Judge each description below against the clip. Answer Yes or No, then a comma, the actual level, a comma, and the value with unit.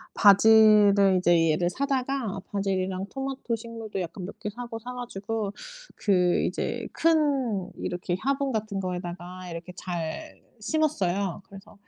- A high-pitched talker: Yes, high, 200 Hz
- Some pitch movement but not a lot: Yes, average, 4.7 semitones